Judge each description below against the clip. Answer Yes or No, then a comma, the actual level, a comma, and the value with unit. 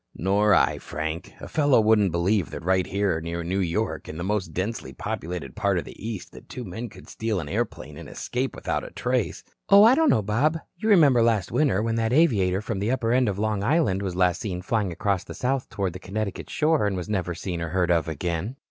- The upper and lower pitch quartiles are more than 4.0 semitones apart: Yes, average, 4.5 semitones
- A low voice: Yes, low, 100 Hz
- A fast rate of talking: Yes, fast, 230 wpm